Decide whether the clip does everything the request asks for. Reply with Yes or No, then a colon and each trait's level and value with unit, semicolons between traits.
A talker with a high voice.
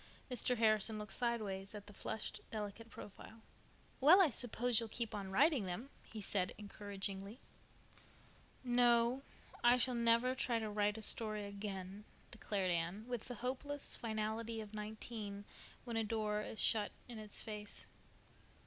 Yes: high, 220 Hz